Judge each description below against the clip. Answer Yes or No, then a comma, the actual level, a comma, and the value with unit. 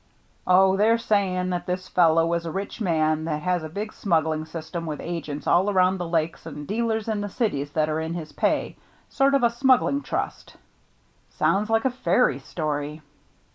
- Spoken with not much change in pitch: No, average, 4.6 semitones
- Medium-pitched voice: Yes, medium, 175 Hz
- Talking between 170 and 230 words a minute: Yes, average, 190 wpm